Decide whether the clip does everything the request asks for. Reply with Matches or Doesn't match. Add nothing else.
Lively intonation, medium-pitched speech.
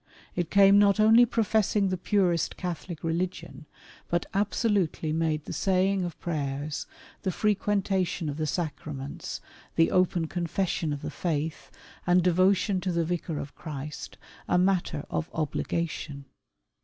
Doesn't match